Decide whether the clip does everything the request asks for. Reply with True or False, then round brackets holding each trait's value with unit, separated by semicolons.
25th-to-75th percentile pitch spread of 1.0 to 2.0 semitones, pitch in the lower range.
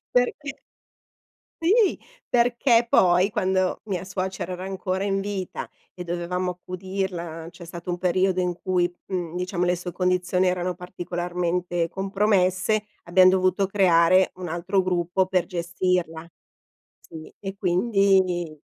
False (1.6 semitones; 185 Hz)